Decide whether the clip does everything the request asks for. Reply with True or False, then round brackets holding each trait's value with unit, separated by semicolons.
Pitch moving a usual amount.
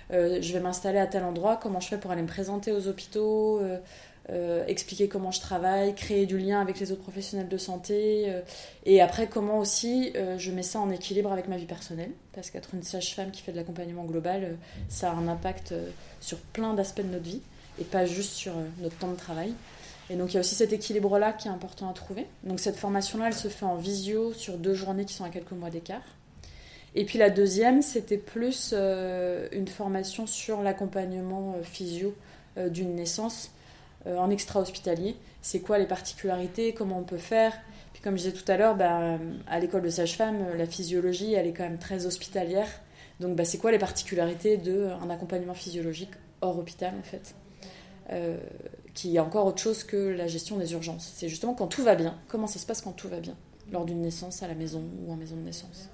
False (2.3 semitones)